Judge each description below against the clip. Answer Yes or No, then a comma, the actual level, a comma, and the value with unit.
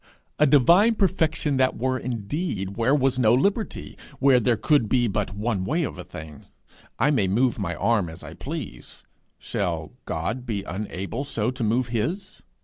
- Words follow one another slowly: No, average, 170 wpm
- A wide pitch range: Yes, wide, 5.9 semitones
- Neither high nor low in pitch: No, low, 120 Hz